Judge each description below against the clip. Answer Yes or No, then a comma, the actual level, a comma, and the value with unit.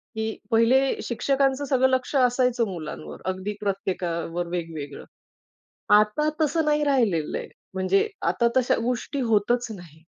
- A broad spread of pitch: Yes, wide, 6.4 semitones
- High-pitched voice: Yes, high, 220 Hz